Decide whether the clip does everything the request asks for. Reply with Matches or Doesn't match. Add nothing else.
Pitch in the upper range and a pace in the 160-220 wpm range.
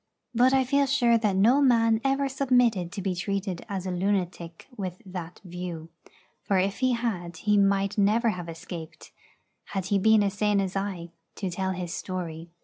Matches